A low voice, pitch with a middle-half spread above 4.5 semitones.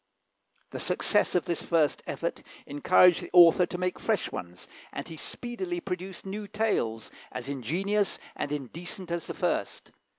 No: medium, 180 Hz; average, 5.2 semitones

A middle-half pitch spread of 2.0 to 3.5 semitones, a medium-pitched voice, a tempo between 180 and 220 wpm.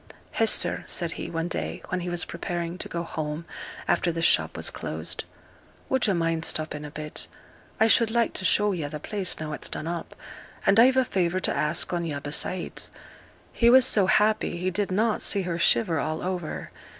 No: average, 4.1 semitones; medium, 175 Hz; average, 200 wpm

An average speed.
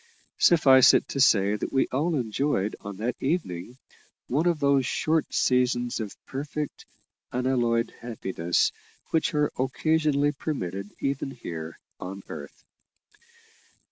No: slow, 120 wpm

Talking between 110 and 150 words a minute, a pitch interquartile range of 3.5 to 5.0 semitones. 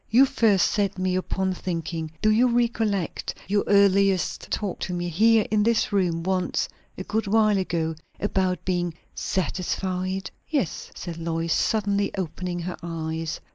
No: average, 145 wpm; average, 3.0 semitones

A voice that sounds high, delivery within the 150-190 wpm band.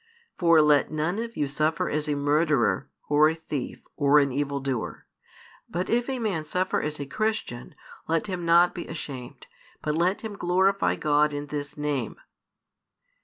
No: medium, 150 Hz; average, 170 wpm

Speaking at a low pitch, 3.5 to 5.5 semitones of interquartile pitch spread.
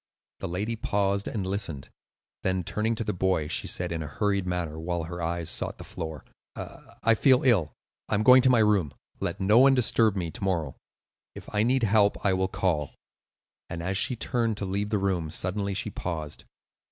Yes: very low, 95 Hz; average, 4.0 semitones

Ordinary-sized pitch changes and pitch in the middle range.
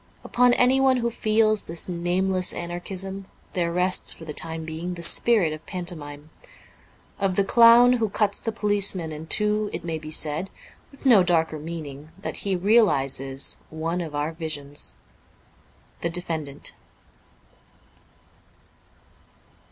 Yes: average, 4.7 semitones; medium, 175 Hz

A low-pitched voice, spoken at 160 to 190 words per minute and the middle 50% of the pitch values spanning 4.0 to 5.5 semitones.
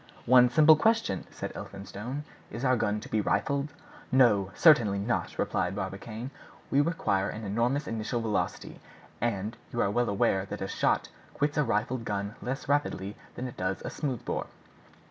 Yes: low, 115 Hz; average, 165 wpm; average, 5.1 semitones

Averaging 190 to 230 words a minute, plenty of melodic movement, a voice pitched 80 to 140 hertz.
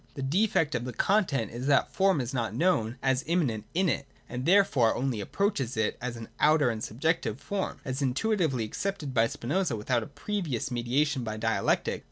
Yes: average, 200 wpm; wide, 6.0 semitones; low, 135 Hz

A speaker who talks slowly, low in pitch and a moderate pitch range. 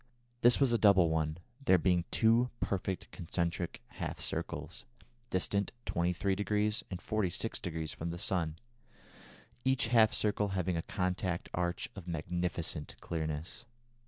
Yes: slow, 125 wpm; very low, 90 Hz; average, 3.4 semitones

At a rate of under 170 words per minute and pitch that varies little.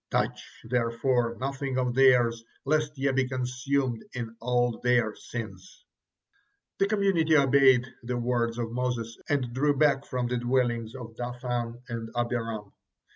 Yes: slow, 135 wpm; narrow, 2.2 semitones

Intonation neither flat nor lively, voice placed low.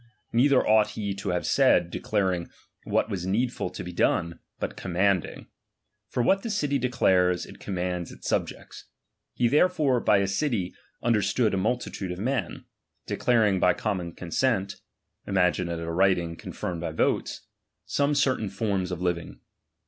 Yes: average, 5.0 semitones; low, 100 Hz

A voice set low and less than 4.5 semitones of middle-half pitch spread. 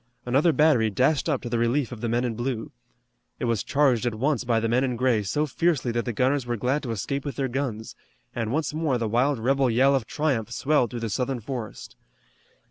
Yes: low, 125 Hz; average, 3.1 semitones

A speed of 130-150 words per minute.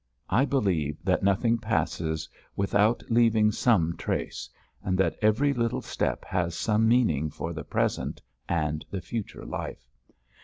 Yes: average, 140 wpm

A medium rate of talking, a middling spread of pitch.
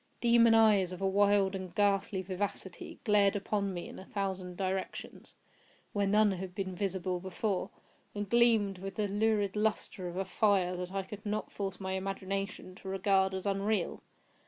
No: average, 170 wpm; narrow, 1.5 semitones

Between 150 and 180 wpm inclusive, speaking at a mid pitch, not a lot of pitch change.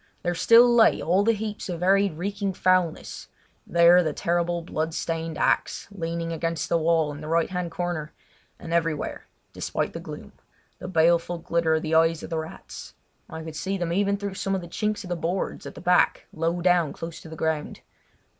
No: average, 200 wpm; medium, 170 Hz; narrow, 2.1 semitones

